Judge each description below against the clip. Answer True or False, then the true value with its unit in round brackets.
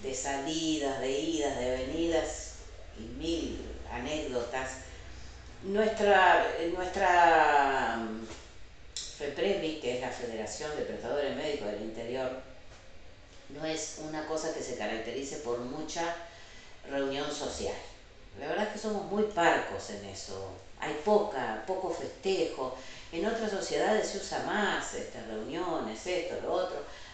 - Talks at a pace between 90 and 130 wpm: True (125 wpm)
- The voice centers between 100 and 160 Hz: True (140 Hz)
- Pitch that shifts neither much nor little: False (7.4 semitones)